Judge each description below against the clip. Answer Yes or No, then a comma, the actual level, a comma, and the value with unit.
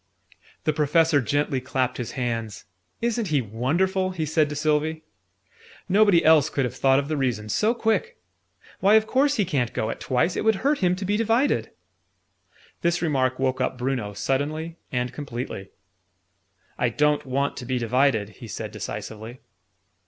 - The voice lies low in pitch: No, medium, 145 Hz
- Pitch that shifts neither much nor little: No, wide, 6.0 semitones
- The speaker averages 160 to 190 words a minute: Yes, average, 165 wpm